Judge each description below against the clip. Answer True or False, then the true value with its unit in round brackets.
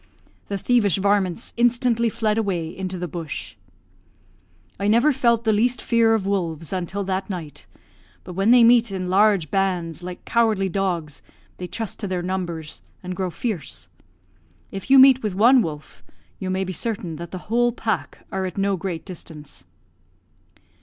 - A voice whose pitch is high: True (195 Hz)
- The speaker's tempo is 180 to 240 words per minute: False (165 wpm)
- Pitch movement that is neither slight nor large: True (4.1 semitones)